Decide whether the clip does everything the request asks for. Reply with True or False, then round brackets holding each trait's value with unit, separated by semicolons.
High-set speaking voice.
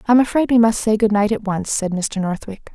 True (215 Hz)